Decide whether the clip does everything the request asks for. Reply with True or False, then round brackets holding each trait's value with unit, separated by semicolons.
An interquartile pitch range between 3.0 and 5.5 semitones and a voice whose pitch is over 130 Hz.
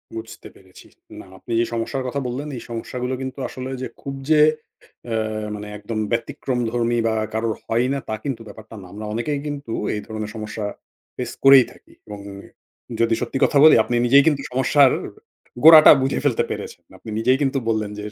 False (3.4 semitones; 120 Hz)